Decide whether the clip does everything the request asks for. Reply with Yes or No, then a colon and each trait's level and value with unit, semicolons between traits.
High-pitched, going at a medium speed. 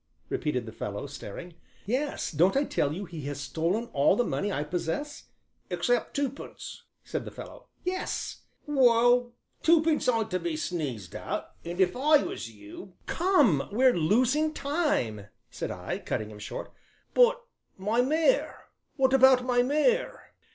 Yes: high, 230 Hz; average, 155 wpm